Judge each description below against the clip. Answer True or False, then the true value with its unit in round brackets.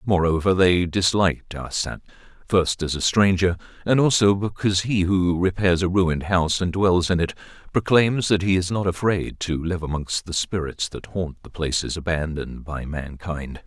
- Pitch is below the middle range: True (90 Hz)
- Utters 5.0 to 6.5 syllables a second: False (4.8 syllables/s)